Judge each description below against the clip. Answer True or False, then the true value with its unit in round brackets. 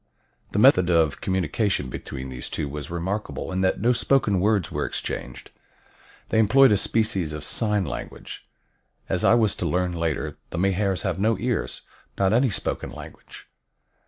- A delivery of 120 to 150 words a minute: False (160 wpm)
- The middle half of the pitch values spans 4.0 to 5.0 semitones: True (4.4 semitones)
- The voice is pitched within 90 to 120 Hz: True (95 Hz)